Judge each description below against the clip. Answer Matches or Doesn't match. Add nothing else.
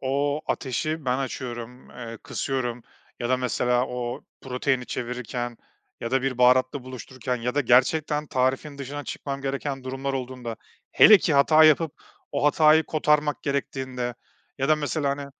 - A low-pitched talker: Matches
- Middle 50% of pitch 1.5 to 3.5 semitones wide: Matches